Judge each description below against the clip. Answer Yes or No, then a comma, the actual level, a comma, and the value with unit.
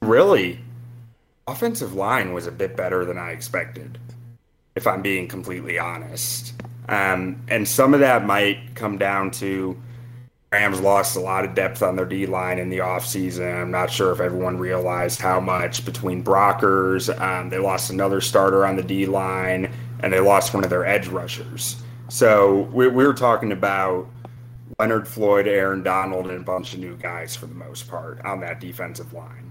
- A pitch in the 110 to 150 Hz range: No, low, 100 Hz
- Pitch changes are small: No, average, 4.5 semitones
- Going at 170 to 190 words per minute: Yes, average, 175 wpm